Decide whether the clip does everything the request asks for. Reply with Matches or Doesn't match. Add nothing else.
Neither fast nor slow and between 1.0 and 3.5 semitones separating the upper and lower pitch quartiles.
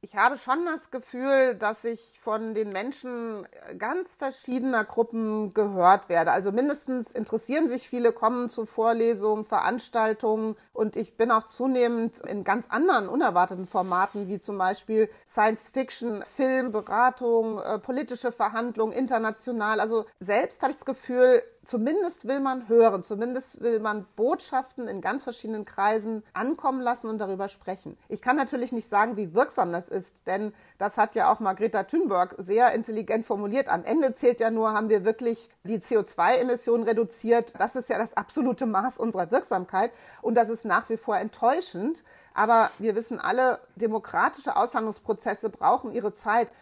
Matches